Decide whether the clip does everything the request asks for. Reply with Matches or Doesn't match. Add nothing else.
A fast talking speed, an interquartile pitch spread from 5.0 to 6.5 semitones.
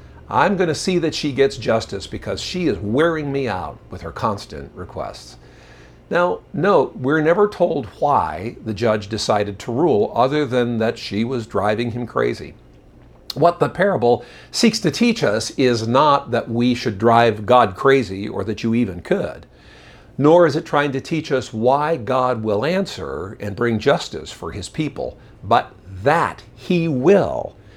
Doesn't match